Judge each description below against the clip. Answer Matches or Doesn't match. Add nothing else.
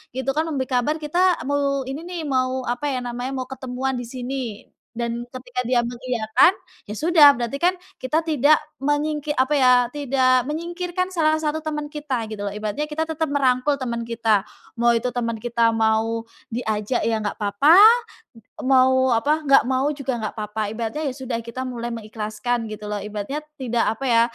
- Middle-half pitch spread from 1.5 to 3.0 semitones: Doesn't match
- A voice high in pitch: Matches